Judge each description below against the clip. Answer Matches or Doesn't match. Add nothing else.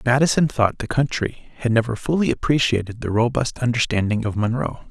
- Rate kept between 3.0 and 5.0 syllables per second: Doesn't match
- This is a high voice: Doesn't match